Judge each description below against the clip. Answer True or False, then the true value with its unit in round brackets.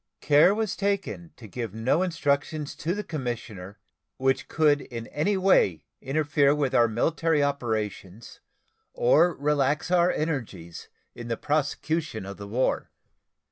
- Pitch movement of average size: False (5.8 semitones)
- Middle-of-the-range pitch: True (145 Hz)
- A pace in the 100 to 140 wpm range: True (135 wpm)